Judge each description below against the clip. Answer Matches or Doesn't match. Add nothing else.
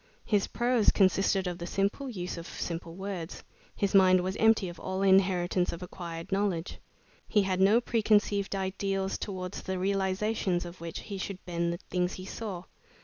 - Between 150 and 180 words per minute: Matches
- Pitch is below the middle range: Doesn't match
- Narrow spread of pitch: Matches